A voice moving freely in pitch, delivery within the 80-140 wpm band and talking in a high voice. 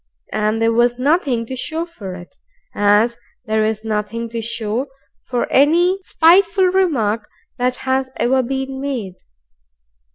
No: average, 4.3 semitones; slow, 135 wpm; high, 245 Hz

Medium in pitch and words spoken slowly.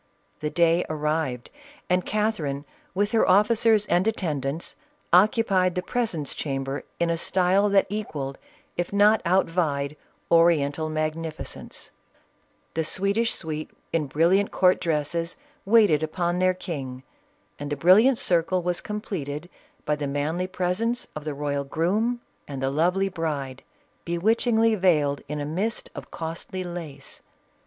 Yes: medium, 170 Hz; slow, 130 wpm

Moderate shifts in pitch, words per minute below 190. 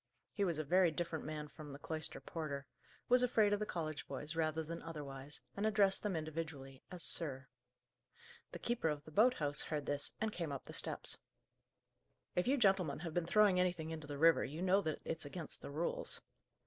No: average, 3.8 semitones; average, 200 wpm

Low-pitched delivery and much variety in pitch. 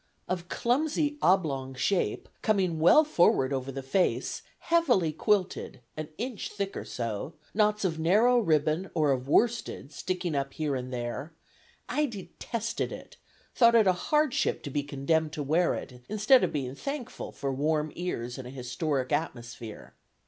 No: medium, 160 Hz; wide, 7.5 semitones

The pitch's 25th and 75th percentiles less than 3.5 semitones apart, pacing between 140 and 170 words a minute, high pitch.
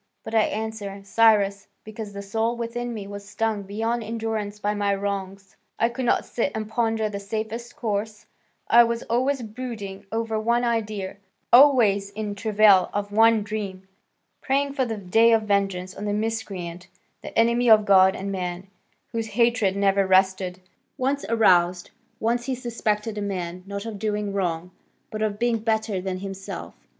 Yes: narrow, 2.5 semitones; average, 165 wpm; high, 210 Hz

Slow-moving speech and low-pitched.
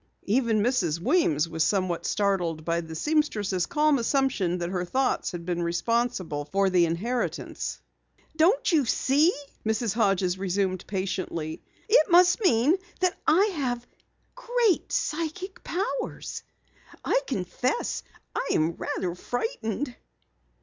No: slow, 120 wpm; high, 220 Hz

